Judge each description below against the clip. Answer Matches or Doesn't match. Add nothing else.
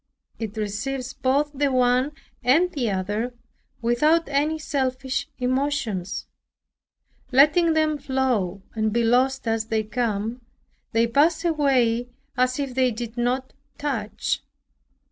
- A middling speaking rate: Doesn't match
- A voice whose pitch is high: Matches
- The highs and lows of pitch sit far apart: Doesn't match